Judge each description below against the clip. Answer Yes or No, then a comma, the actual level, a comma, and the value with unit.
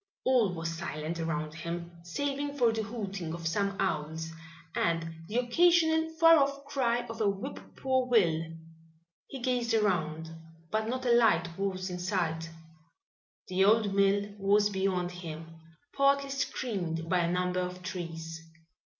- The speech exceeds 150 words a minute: No, average, 145 wpm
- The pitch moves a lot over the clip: Yes, wide, 6.2 semitones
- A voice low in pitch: No, high, 195 Hz